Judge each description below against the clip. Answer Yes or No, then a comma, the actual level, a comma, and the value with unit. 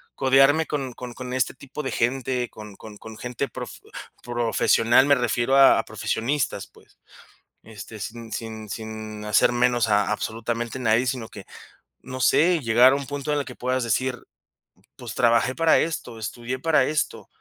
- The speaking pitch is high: No, low, 125 Hz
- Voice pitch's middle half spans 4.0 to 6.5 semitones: No, average, 3.0 semitones